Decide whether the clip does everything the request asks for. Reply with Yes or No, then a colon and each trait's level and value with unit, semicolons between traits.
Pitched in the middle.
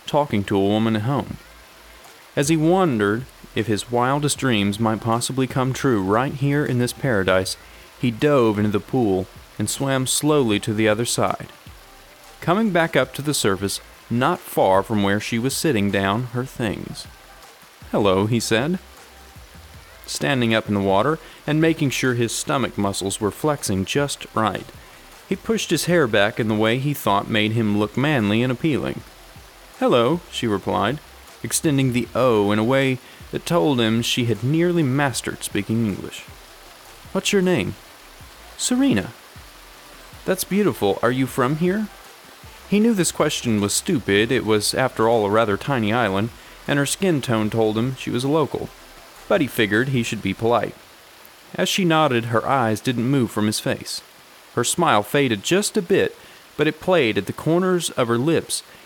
No: low, 120 Hz